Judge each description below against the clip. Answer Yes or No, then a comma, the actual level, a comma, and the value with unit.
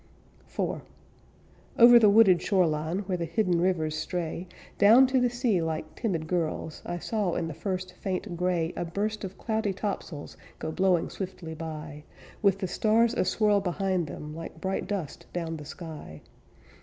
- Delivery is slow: No, average, 165 wpm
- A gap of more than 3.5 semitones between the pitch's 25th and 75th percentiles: Yes, average, 3.9 semitones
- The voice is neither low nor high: Yes, medium, 180 Hz